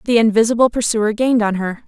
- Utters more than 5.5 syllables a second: Yes, 6.4 syllables/s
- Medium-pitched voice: No, high, 225 Hz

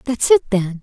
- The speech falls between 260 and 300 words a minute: No, fast, 215 wpm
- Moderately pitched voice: No, high, 230 Hz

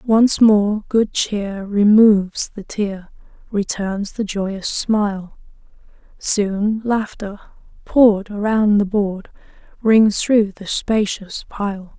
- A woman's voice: Yes, female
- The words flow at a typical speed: No, slow, 110 wpm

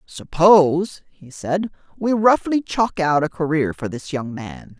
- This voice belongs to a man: Yes, male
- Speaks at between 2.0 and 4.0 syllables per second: Yes, 3.9 syllables/s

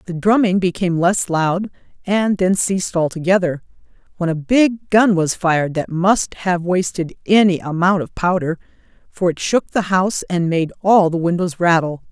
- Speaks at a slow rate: No, average, 170 wpm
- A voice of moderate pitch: Yes, medium, 180 Hz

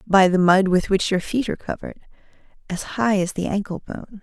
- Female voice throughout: Yes, female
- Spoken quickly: Yes, fast, 215 wpm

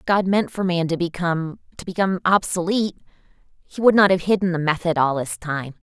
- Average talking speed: Yes, average, 195 wpm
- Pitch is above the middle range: No, medium, 175 Hz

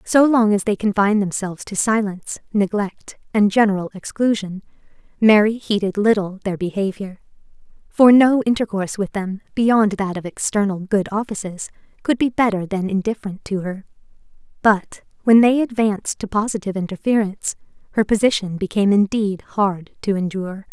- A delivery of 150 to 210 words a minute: No, average, 140 wpm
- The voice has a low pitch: No, high, 205 Hz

